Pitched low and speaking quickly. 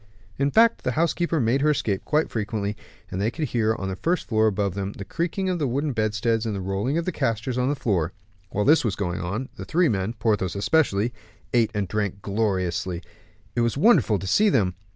Yes: low, 110 Hz; fast, 215 wpm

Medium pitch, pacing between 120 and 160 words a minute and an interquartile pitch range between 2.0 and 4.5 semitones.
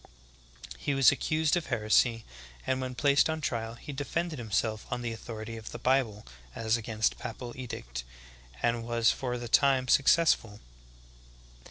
No: low, 120 Hz; average, 155 wpm; average, 3.3 semitones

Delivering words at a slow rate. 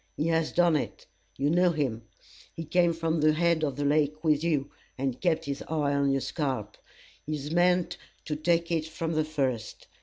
No: average, 195 wpm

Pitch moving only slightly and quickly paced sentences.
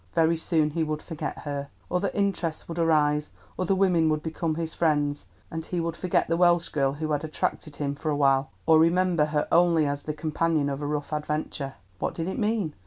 Yes: narrow, 2.1 semitones; fast, 210 wpm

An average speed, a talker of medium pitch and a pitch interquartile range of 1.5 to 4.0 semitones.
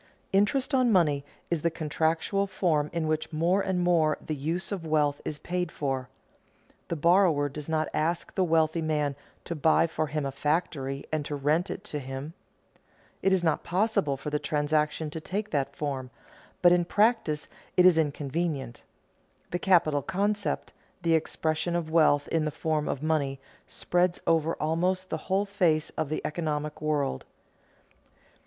Yes: average, 165 wpm; medium, 160 Hz; average, 3.0 semitones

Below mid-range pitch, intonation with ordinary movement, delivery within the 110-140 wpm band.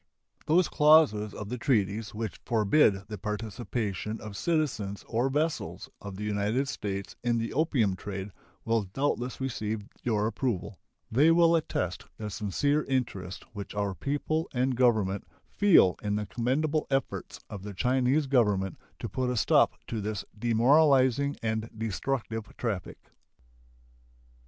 Yes: low, 115 Hz; average, 4.6 semitones; slow, 135 wpm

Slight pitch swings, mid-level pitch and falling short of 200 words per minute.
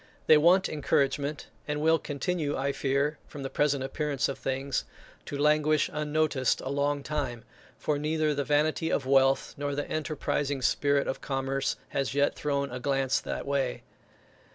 Yes: narrow, 1.7 semitones; medium, 145 Hz; average, 160 wpm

